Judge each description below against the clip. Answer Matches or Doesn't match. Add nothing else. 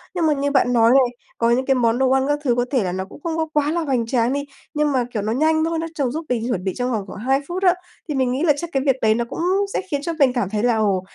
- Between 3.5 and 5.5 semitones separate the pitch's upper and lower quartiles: Matches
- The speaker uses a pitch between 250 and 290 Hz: Matches